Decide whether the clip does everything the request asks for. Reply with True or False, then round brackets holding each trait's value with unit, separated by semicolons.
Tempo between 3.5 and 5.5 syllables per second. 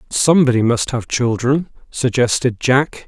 True (4.5 syllables/s)